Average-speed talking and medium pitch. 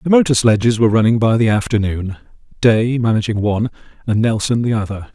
No: average, 175 wpm; low, 110 Hz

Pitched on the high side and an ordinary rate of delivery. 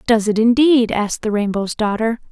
Yes: high, 225 Hz; average, 180 wpm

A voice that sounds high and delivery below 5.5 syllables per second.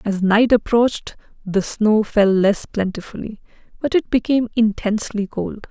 Yes: high, 215 Hz; 4.7 syllables/s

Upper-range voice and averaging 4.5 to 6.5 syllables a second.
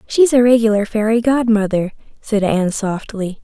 Yes: high, 220 Hz; 5.0 syllables/s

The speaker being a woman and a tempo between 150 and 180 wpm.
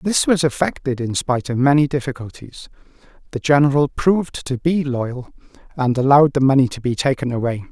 No: male; average, 170 wpm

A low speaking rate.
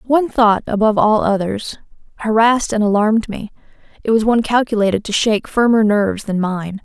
No: average, 165 wpm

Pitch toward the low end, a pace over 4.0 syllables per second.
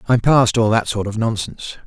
Yes: low, 115 Hz; 5.6 syllables/s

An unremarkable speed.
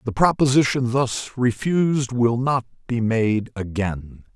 No: slow, 125 wpm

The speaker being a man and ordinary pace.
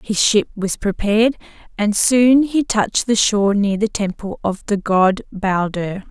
No: female; average, 165 wpm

